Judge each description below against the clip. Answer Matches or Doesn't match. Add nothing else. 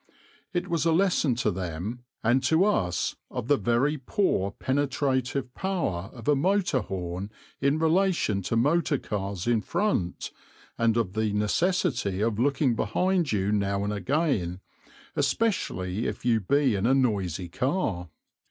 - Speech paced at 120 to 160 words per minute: Matches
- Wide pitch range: Matches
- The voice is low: Matches